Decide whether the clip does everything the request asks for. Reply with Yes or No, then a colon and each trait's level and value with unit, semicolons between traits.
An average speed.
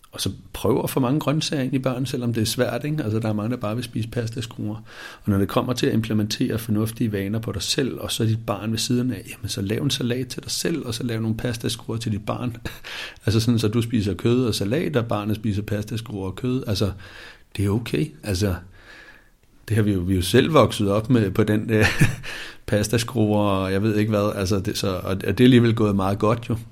No: fast, 255 wpm